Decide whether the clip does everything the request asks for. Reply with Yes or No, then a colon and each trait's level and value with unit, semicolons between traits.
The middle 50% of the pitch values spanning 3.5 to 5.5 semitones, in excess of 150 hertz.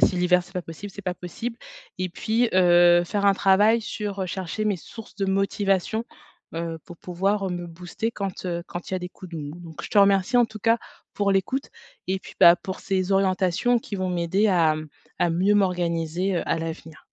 No: narrow, 2.5 semitones; medium, 185 Hz